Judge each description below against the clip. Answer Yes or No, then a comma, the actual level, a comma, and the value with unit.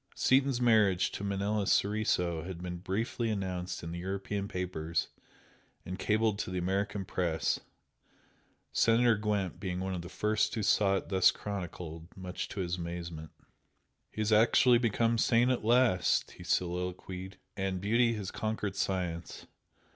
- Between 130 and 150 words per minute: Yes, average, 145 wpm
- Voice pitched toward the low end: Yes, very low, 95 Hz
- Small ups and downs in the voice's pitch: No, average, 3.3 semitones